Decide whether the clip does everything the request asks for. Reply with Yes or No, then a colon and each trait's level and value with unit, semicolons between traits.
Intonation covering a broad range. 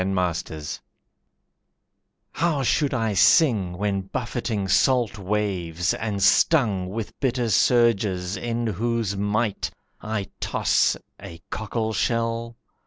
No: average, 3.5 semitones